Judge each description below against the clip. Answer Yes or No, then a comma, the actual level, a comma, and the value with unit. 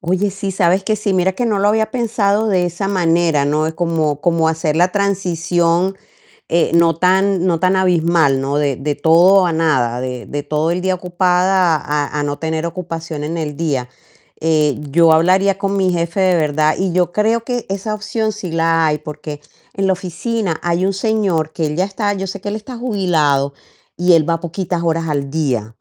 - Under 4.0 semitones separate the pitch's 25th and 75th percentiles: Yes, average, 3.5 semitones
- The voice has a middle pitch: Yes, medium, 175 Hz